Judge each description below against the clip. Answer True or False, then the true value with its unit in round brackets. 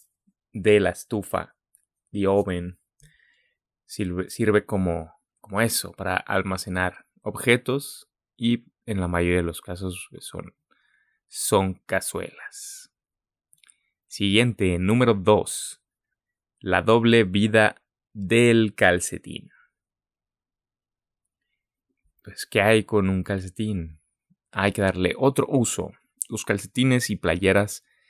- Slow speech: True (100 wpm)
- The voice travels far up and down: False (3.5 semitones)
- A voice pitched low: True (100 Hz)